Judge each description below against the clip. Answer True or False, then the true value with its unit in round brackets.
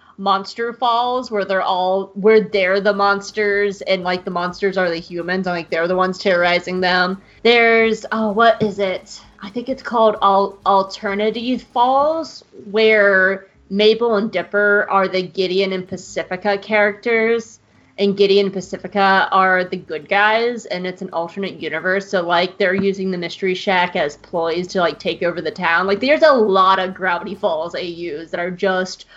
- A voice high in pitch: True (195 Hz)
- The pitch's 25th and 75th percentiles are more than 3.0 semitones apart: False (2.5 semitones)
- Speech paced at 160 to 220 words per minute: True (175 wpm)